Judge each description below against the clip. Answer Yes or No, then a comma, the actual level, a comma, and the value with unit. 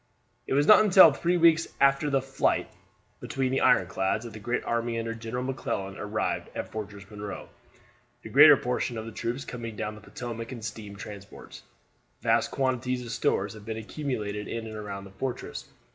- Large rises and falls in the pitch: No, average, 3.8 semitones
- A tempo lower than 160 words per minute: No, average, 180 wpm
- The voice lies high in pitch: No, low, 115 Hz